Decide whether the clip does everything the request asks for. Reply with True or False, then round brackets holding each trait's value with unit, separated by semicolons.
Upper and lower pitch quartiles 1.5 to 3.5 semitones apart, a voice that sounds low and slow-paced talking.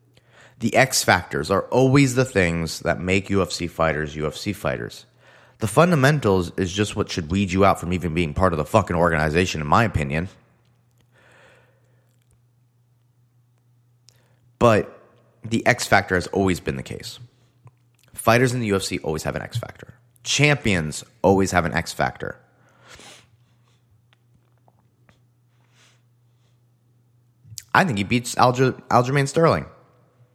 False (4.6 semitones; 120 Hz; 125 wpm)